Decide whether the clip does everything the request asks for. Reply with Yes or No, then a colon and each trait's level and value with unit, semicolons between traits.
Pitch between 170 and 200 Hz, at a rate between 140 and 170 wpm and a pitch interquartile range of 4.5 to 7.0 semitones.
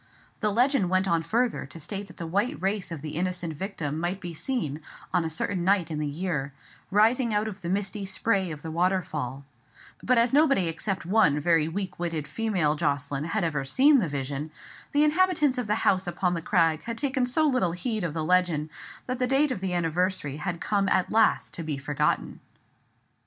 No: medium, 185 Hz; average, 200 wpm; average, 5.3 semitones